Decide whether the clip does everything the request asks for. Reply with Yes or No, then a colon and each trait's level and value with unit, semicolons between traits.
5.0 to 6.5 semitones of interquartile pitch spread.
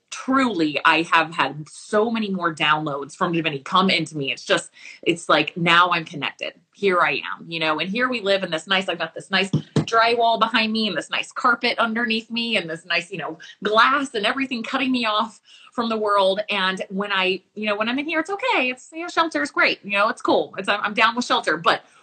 Yes: wide, 5.5 semitones